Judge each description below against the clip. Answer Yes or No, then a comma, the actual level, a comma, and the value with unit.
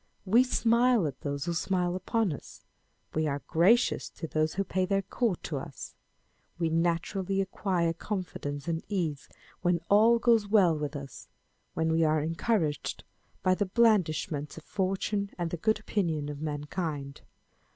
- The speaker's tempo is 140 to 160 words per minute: Yes, average, 155 wpm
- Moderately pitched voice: Yes, medium, 175 Hz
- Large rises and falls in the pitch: No, average, 4.4 semitones